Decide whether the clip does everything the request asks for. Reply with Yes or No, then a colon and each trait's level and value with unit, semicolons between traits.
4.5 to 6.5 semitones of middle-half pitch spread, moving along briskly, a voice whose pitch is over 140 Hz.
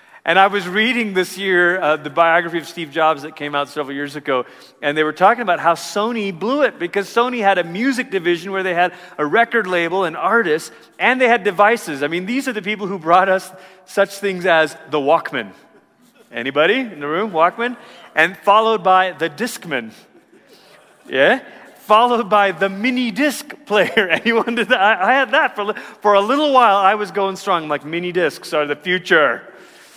No: average, 4.9 semitones; average, 195 wpm; high, 190 Hz